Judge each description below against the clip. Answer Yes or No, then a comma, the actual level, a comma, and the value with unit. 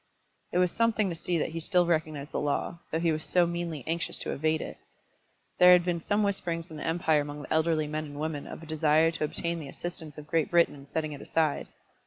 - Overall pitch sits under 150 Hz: No, medium, 160 Hz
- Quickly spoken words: Yes, fast, 240 wpm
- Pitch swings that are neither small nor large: No, narrow, 2.0 semitones